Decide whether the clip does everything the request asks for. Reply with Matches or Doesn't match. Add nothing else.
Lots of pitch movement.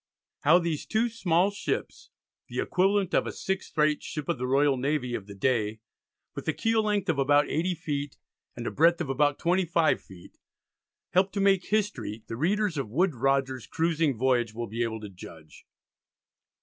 Matches